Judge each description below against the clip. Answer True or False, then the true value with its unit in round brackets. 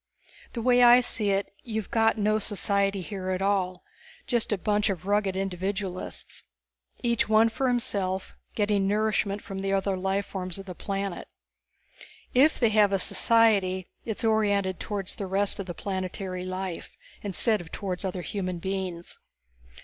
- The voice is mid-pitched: False (200 Hz)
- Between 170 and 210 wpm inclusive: False (160 wpm)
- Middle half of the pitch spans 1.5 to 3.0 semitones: True (2.4 semitones)